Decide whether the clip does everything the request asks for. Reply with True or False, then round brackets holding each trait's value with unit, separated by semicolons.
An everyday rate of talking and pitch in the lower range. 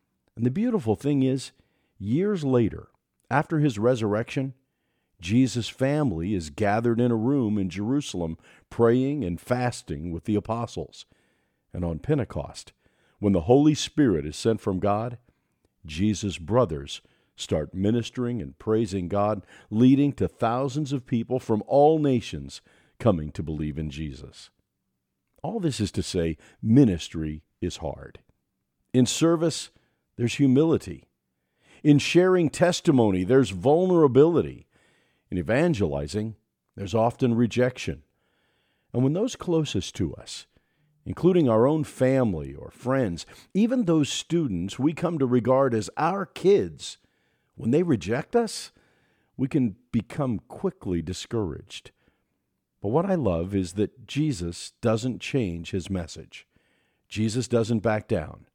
False (125 wpm; 120 Hz)